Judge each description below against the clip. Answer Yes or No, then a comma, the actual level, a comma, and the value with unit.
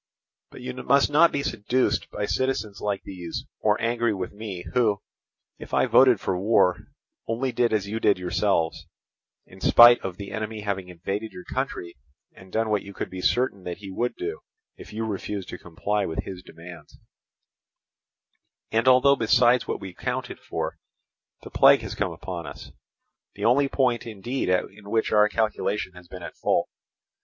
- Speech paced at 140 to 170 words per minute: Yes, average, 165 wpm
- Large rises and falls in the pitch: No, average, 4.3 semitones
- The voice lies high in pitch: No, low, 105 Hz